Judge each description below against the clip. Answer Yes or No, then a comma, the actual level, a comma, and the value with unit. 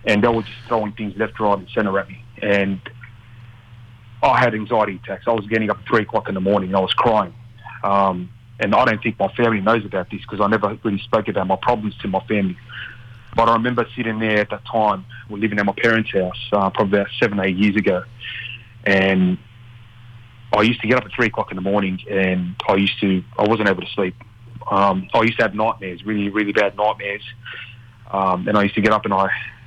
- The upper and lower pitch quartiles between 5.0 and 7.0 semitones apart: No, average, 2.7 semitones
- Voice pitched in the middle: No, low, 110 Hz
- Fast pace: Yes, fast, 230 wpm